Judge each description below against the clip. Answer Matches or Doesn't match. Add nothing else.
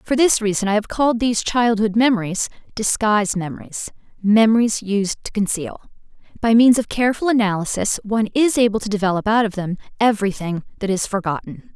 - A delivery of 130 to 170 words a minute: Matches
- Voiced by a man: Doesn't match